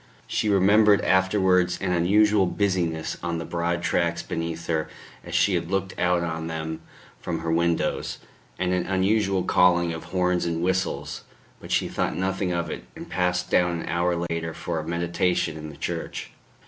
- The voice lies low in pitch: Yes, very low, 85 Hz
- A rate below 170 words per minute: No, average, 175 wpm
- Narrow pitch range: Yes, narrow, 2.0 semitones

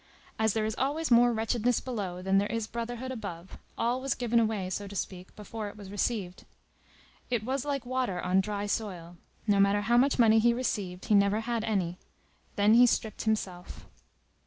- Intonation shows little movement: No, average, 3.2 semitones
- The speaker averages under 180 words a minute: No, average, 185 wpm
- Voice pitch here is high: Yes, high, 220 Hz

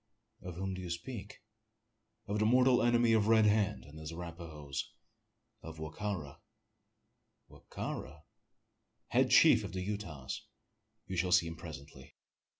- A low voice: Yes, very low, 90 Hz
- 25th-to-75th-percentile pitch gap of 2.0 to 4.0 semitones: No, average, 5.0 semitones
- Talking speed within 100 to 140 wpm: No, average, 150 wpm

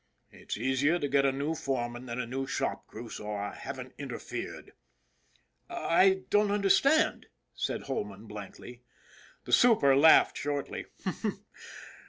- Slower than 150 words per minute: Yes, average, 140 wpm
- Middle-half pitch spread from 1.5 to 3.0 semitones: No, average, 5.0 semitones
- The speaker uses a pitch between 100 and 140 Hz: Yes, low, 135 Hz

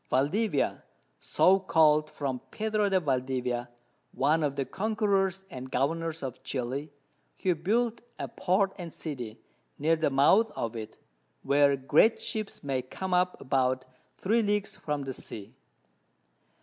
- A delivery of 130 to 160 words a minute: Yes, slow, 135 wpm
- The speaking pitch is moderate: Yes, medium, 155 Hz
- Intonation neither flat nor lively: No, wide, 6.5 semitones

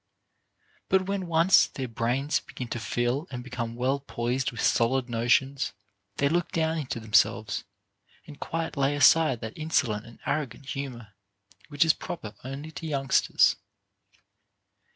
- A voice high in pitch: No, low, 135 Hz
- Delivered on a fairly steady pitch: No, average, 4.3 semitones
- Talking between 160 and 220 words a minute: No, average, 140 wpm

